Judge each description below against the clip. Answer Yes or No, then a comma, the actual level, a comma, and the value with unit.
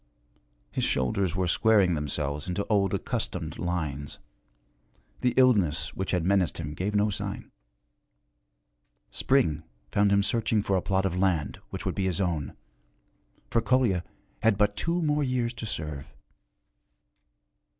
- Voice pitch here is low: Yes, very low, 95 Hz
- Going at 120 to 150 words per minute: Yes, slow, 135 wpm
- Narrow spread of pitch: No, average, 4.6 semitones